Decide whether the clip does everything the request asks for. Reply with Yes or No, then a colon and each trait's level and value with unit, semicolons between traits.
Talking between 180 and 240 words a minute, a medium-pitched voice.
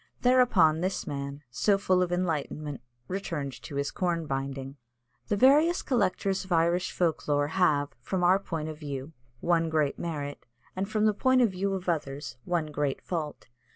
No: average, 170 wpm; medium, 165 Hz